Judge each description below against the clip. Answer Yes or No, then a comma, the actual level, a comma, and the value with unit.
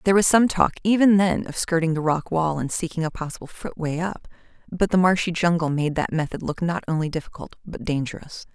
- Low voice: No, medium, 170 Hz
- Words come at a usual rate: No, fast, 210 wpm